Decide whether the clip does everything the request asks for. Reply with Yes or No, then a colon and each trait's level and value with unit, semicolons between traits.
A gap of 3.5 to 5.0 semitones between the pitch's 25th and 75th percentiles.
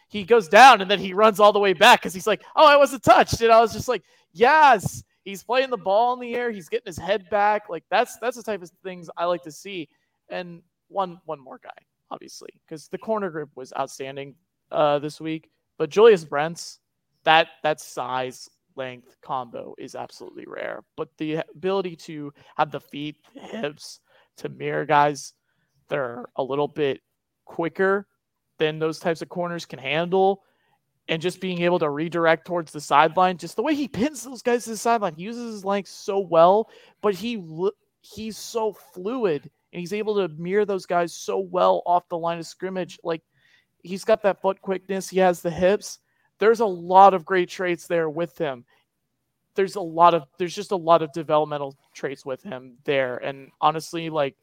Yes: average, 4.6 semitones